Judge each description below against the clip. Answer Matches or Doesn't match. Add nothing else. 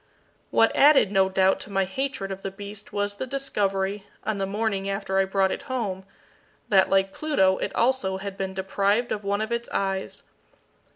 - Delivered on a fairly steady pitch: Matches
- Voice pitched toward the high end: Matches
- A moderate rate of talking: Matches